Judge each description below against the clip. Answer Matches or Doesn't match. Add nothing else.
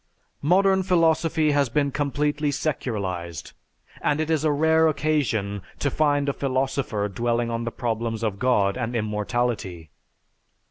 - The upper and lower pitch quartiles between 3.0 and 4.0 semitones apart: Doesn't match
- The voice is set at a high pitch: Doesn't match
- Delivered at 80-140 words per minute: Matches